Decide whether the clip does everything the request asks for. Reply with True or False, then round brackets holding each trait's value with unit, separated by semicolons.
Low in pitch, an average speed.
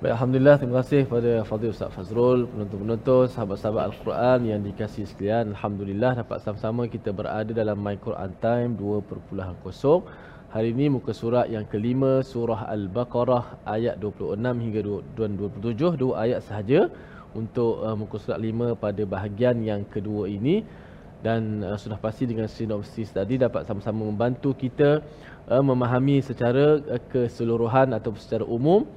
False (115 Hz; 130 wpm)